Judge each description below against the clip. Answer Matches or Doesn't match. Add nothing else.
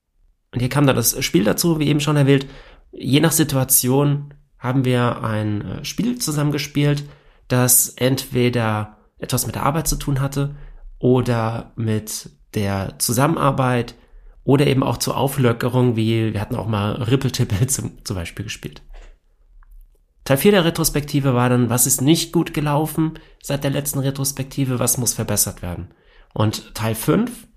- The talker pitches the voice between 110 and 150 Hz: Matches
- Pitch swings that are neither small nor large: Matches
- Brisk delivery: Doesn't match